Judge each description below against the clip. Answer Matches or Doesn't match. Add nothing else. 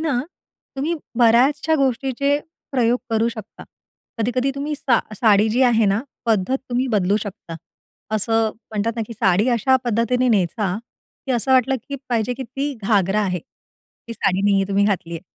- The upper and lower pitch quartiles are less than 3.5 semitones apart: Doesn't match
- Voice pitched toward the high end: Matches